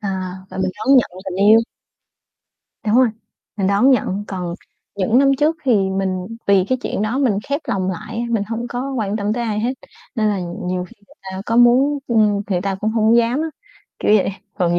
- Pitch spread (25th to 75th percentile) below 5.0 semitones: Yes, average, 4.0 semitones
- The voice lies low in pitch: No, high, 215 Hz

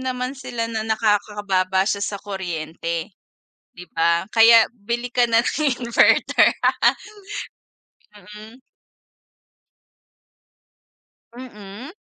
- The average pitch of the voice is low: No, high, 215 Hz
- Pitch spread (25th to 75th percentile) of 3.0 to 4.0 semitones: Yes, average, 3.7 semitones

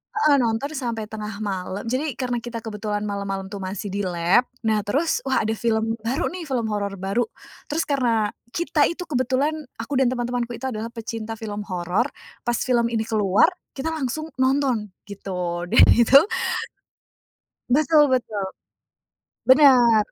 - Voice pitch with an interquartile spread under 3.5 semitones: No, average, 4.0 semitones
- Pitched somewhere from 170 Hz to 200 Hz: No, high, 230 Hz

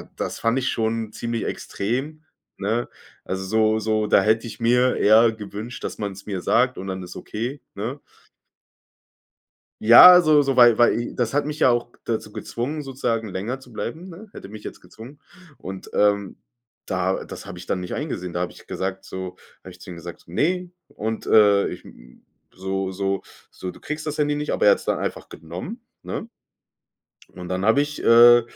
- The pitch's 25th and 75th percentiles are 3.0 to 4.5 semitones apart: No, average, 5.1 semitones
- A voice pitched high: No, low, 110 Hz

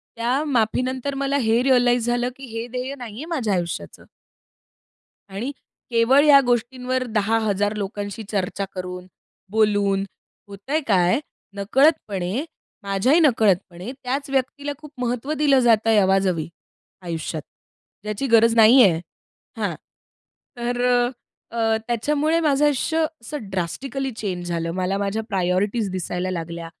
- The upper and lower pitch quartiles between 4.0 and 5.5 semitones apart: Yes, average, 5.0 semitones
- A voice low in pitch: No, high, 225 Hz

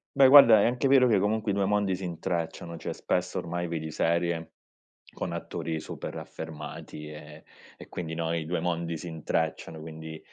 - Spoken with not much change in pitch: No, average, 3.4 semitones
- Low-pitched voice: Yes, very low, 85 Hz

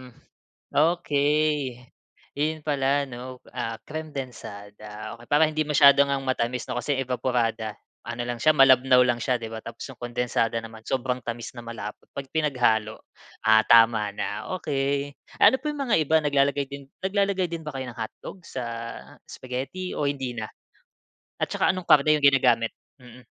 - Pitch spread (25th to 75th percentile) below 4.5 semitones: Yes, average, 3.8 semitones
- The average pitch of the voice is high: No, low, 130 Hz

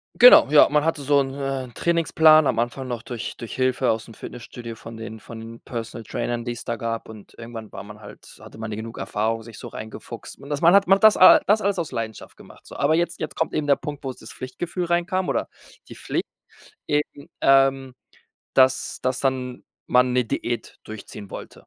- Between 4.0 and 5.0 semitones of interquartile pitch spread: Yes, average, 4.4 semitones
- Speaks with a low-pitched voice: Yes, low, 130 Hz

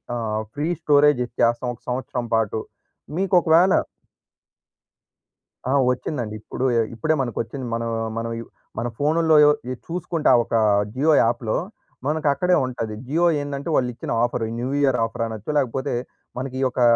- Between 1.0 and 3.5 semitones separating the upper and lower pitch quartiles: No, average, 4.3 semitones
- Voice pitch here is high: No, low, 130 Hz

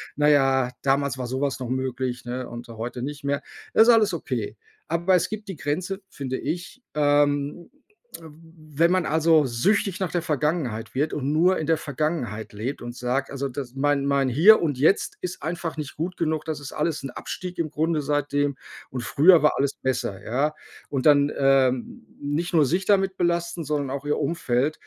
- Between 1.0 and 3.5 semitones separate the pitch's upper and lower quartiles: No, average, 3.9 semitones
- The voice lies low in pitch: No, medium, 145 Hz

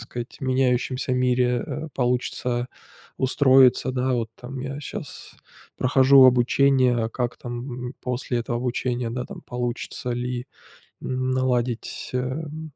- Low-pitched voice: Yes, low, 125 Hz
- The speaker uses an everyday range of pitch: No, narrow, 1.2 semitones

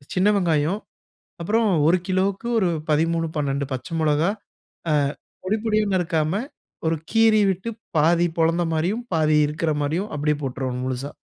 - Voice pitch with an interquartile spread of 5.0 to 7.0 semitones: No, average, 4.1 semitones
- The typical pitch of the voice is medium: Yes, medium, 165 Hz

